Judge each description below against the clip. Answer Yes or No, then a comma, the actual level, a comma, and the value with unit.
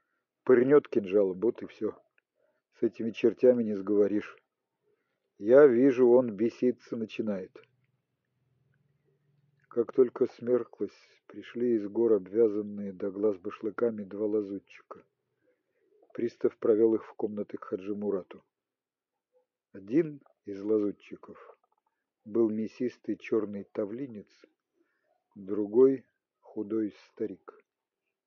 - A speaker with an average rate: No, slow, 95 wpm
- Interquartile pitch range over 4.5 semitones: Yes, average, 5.2 semitones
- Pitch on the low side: Yes, low, 120 Hz